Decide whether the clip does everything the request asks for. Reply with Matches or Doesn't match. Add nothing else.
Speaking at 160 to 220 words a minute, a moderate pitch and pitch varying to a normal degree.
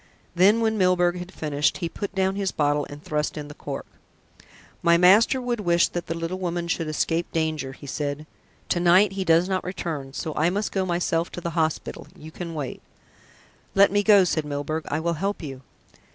Matches